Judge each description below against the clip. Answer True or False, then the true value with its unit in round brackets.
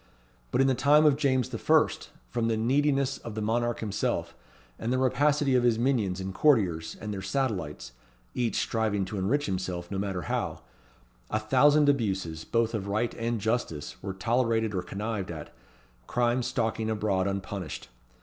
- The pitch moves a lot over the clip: False (4.7 semitones)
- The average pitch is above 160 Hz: False (110 Hz)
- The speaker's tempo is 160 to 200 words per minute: True (170 wpm)